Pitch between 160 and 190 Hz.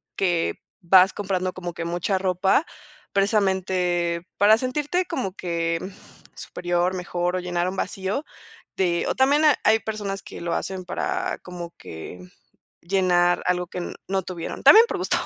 Yes: medium, 185 Hz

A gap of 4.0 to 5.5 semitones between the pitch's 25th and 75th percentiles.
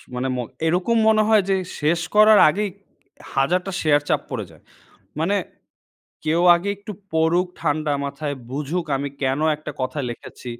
Yes: average, 4.4 semitones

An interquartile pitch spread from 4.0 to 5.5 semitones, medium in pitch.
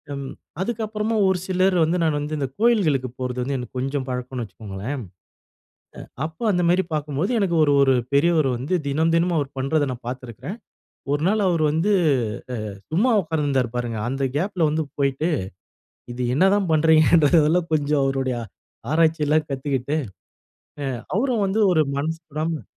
Yes: average, 4.3 semitones; medium, 150 Hz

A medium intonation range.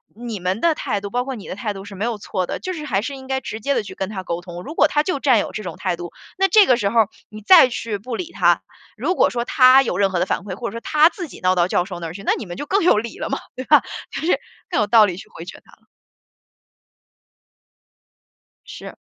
No: wide, 5.8 semitones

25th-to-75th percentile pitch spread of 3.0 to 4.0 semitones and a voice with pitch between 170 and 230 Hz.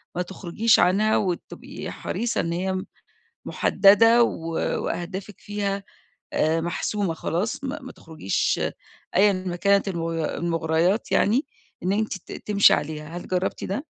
Yes: average, 3.5 semitones; high, 190 Hz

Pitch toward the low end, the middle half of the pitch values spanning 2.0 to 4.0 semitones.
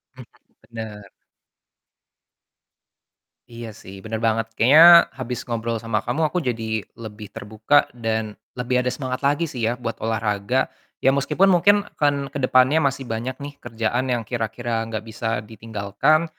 Yes: low, 120 Hz; average, 3.2 semitones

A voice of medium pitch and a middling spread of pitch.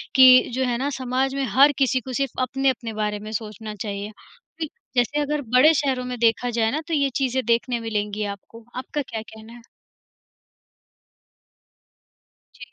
No: high, 245 Hz; average, 3.3 semitones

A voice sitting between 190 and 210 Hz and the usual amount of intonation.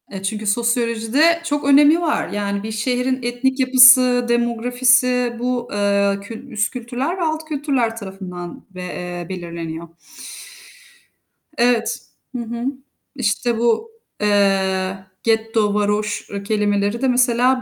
No: high, 235 Hz; average, 3.8 semitones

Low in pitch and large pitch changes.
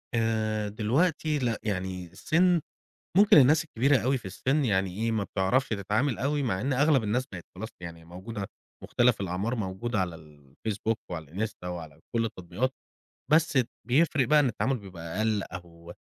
Yes: low, 110 Hz; wide, 5.9 semitones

